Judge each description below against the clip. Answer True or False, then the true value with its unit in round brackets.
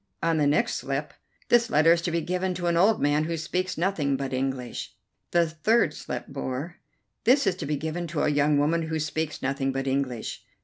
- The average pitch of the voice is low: False (155 Hz)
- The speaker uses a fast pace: True (210 wpm)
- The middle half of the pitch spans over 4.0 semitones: False (3.5 semitones)